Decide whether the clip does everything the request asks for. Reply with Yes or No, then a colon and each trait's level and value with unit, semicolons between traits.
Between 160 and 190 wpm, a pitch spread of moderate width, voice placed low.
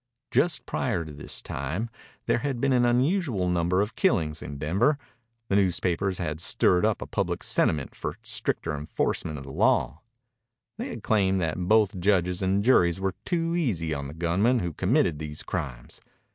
No: average, 170 wpm; wide, 6.5 semitones; very low, 95 Hz